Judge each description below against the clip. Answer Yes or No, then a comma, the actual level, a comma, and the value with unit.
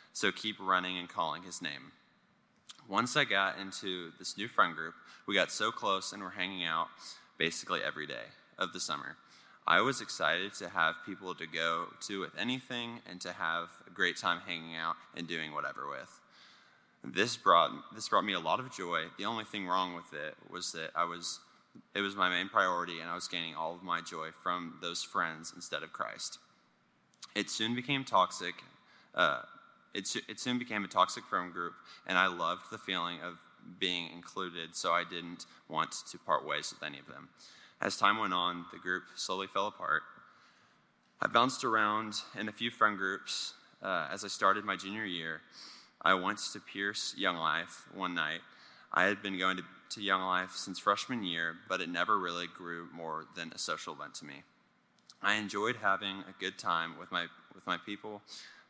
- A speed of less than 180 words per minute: No, average, 190 wpm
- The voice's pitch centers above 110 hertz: No, very low, 90 Hz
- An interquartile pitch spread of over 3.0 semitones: No, average, 2.7 semitones